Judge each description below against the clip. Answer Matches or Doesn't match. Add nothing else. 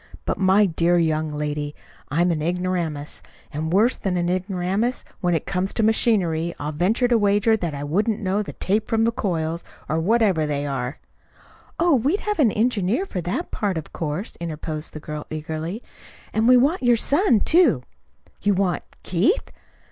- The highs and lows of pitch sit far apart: Matches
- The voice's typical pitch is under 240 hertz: Matches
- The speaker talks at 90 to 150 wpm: Doesn't match